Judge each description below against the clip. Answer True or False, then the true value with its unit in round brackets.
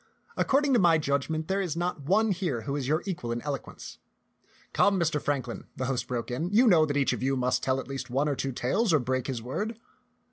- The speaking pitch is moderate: True (145 Hz)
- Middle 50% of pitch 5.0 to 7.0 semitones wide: True (5.5 semitones)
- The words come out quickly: True (245 wpm)